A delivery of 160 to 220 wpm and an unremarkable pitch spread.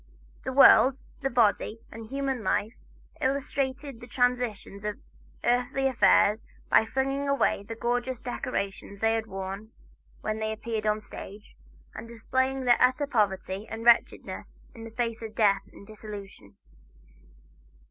No: average, 140 wpm; average, 3.4 semitones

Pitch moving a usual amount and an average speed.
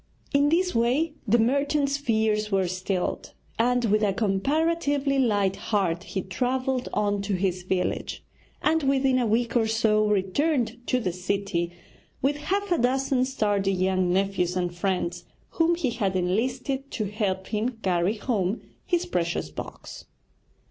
No: wide, 5.8 semitones; average, 150 wpm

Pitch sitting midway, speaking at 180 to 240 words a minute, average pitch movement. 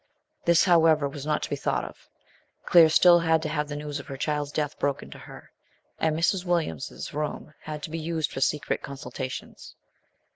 No: medium, 150 Hz; average, 190 wpm; narrow, 2.2 semitones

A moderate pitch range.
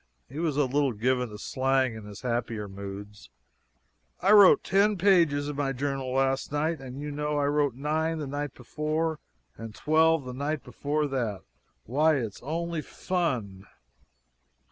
Yes: average, 3.8 semitones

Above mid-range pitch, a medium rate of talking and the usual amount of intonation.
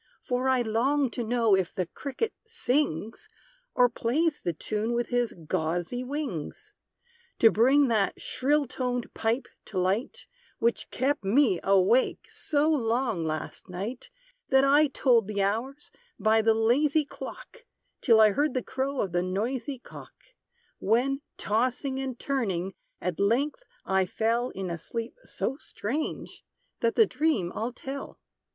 Yes: high, 240 Hz; average, 145 wpm; average, 4.7 semitones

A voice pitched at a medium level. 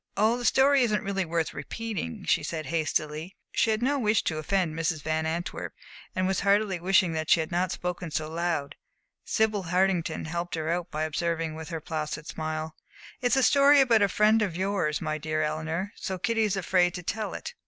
Yes: medium, 175 Hz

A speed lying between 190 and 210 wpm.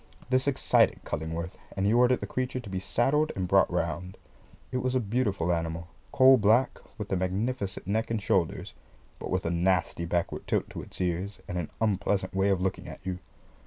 Yes: average, 195 wpm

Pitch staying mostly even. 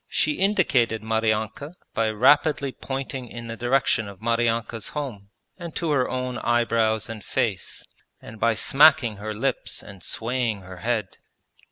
No: average, 3.4 semitones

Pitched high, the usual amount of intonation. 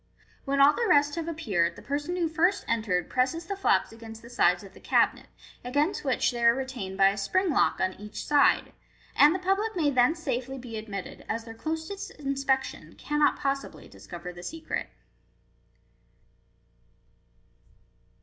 No: very high, 275 Hz; wide, 6.1 semitones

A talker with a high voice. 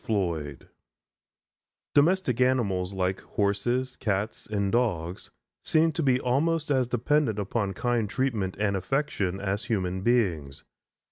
No: low, 110 Hz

